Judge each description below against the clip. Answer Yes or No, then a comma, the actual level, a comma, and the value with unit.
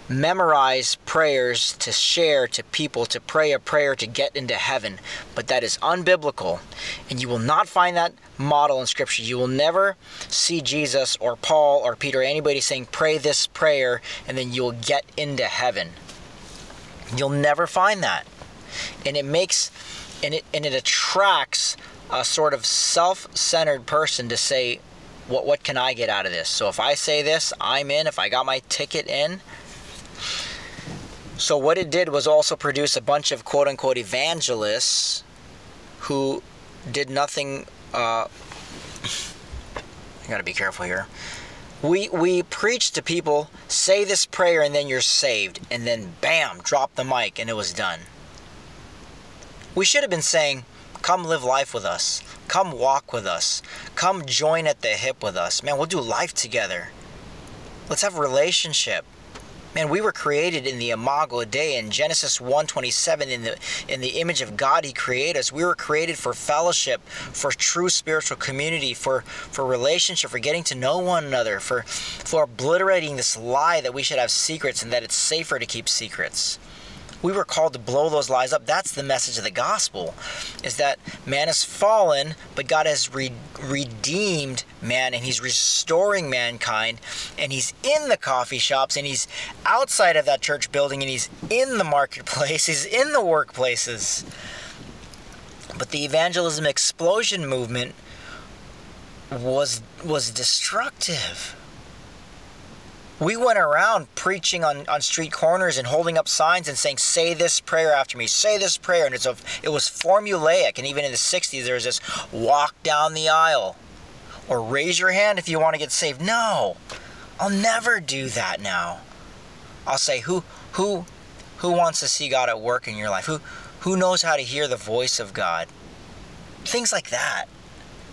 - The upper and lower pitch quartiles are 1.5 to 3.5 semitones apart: No, average, 4.8 semitones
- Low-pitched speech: No, medium, 150 Hz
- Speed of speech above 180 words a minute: No, average, 170 wpm